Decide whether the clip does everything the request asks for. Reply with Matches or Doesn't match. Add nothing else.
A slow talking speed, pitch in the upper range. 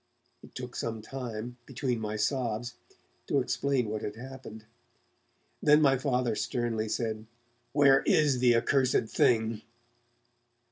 Doesn't match